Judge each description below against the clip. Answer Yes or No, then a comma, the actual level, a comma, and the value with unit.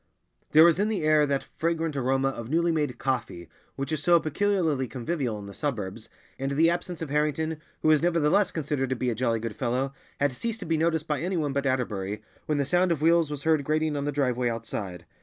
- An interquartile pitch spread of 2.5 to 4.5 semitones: Yes, average, 4.1 semitones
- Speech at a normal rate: No, fast, 220 wpm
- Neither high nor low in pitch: Yes, medium, 145 Hz